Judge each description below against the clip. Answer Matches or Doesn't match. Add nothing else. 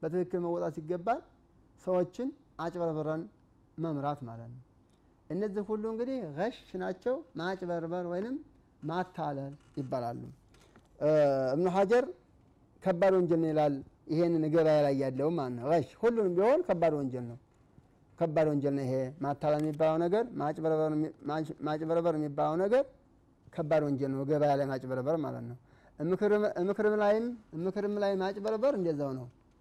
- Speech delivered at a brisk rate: Matches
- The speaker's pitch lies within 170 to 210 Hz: Doesn't match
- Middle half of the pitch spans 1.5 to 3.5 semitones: Doesn't match